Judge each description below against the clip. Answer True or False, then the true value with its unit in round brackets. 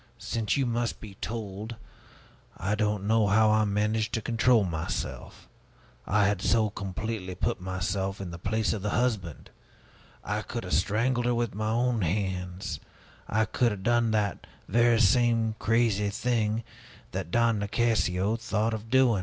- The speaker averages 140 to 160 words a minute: True (155 wpm)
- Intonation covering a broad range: False (2.8 semitones)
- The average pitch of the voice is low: True (110 Hz)